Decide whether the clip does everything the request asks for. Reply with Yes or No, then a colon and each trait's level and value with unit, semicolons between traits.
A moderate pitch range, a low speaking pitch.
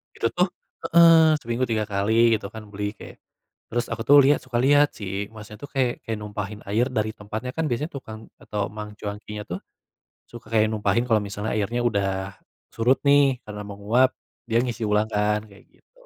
Yes: average, 3.1 semitones; low, 110 Hz